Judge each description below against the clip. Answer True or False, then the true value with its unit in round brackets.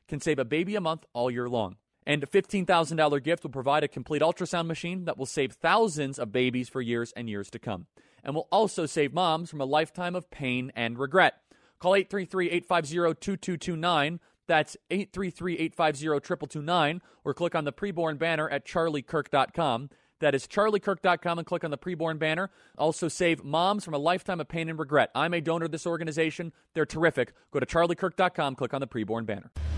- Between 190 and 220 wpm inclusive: False (180 wpm)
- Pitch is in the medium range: True (160 Hz)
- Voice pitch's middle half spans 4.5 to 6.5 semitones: False (3.7 semitones)